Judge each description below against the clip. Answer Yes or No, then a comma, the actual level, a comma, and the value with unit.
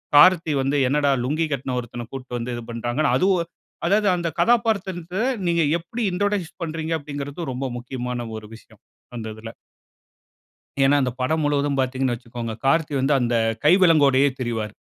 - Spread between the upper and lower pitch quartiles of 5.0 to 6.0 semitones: Yes, average, 5.3 semitones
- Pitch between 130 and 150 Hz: Yes, medium, 140 Hz